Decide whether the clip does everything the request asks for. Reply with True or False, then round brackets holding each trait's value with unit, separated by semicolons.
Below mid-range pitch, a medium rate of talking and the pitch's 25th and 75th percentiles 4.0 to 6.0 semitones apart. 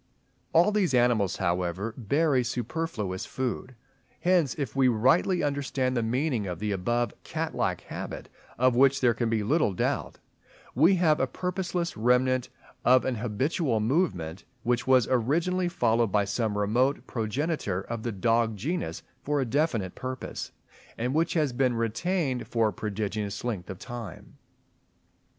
True (125 Hz; 150 wpm; 4.9 semitones)